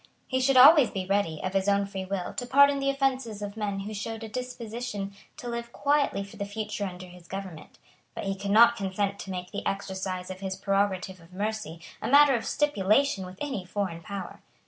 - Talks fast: Yes, fast, 210 wpm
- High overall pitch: Yes, high, 200 Hz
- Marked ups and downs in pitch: No, average, 3.8 semitones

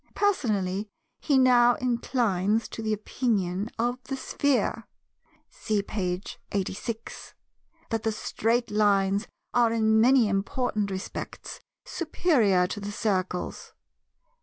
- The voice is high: Yes, high, 220 Hz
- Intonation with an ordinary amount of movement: Yes, average, 3.5 semitones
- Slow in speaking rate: Yes, slow, 110 wpm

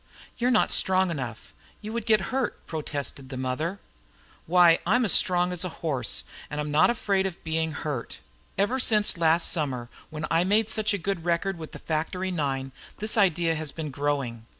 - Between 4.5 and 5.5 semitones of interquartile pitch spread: Yes, average, 4.8 semitones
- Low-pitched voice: No, medium, 165 Hz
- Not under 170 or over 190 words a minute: Yes, average, 180 wpm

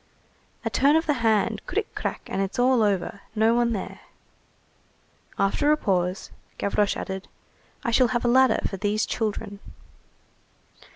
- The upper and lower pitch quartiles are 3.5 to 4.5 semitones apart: Yes, average, 3.8 semitones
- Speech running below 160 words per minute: Yes, average, 150 wpm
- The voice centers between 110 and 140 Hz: No, high, 220 Hz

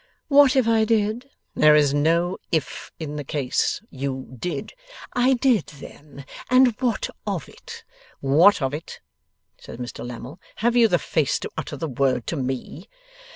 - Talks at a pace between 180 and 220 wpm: No, average, 160 wpm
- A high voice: No, medium, 160 Hz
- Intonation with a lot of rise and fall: Yes, wide, 8.6 semitones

